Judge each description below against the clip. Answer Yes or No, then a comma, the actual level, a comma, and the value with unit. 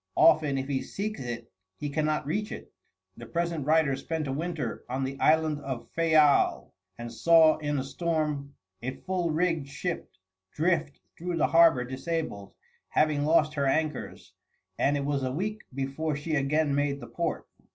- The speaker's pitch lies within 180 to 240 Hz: No, medium, 150 Hz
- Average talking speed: Yes, average, 165 wpm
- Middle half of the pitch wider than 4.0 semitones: No, average, 3.1 semitones